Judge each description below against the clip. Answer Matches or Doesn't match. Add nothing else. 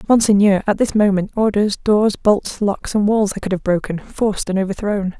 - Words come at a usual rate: Matches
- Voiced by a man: Doesn't match